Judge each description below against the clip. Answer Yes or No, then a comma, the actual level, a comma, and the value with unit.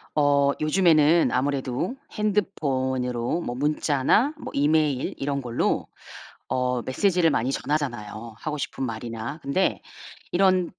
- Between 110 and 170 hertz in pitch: Yes, medium, 140 Hz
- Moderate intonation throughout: Yes, average, 4.4 semitones